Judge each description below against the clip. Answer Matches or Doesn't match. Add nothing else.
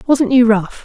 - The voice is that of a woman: Matches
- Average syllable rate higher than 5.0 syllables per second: Doesn't match